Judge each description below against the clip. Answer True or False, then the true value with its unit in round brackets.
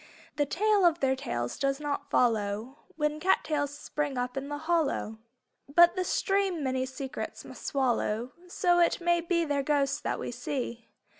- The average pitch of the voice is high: True (290 Hz)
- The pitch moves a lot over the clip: False (4.6 semitones)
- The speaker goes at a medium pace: True (170 wpm)